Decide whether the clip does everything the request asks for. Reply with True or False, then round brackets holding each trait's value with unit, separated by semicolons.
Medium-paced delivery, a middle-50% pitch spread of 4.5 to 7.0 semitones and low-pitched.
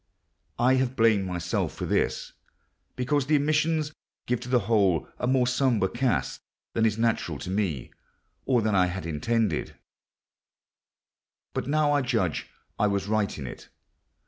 True (150 wpm; 5.4 semitones; 115 Hz)